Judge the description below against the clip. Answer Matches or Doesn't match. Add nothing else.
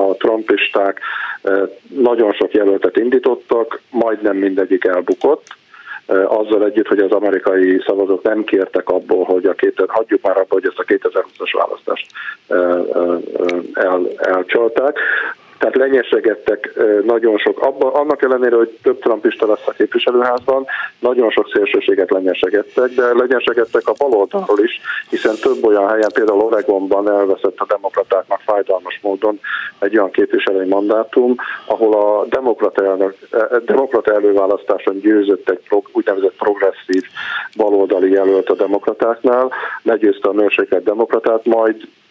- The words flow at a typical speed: Matches